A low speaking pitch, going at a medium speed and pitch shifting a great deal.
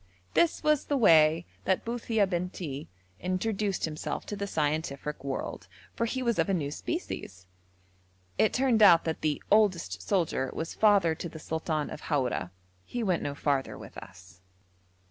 No: medium, 170 Hz; average, 160 wpm; wide, 6.1 semitones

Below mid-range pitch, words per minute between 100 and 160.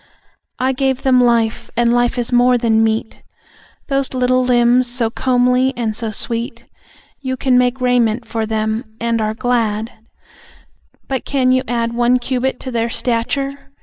No: high, 245 Hz; average, 155 wpm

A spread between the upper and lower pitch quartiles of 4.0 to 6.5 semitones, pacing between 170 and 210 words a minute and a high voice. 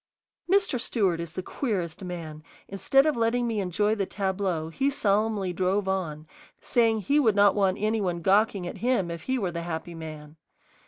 Yes: average, 4.4 semitones; average, 180 wpm; high, 195 Hz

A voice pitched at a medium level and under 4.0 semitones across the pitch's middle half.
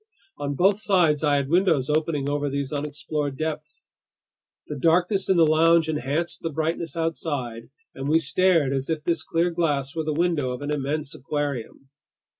Yes: medium, 150 Hz; average, 2.7 semitones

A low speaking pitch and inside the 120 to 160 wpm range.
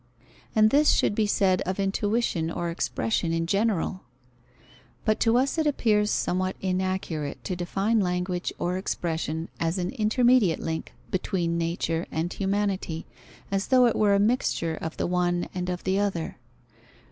No: medium, 185 Hz; average, 155 wpm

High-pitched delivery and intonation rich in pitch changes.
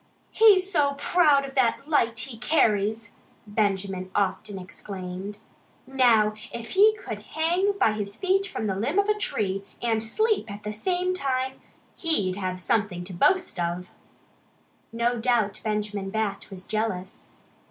Yes: high, 220 Hz; wide, 6.8 semitones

